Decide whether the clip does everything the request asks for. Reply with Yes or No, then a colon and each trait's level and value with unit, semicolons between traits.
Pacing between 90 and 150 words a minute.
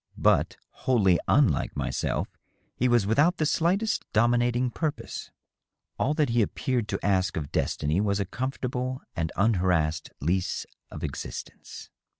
Yes: slow, 135 wpm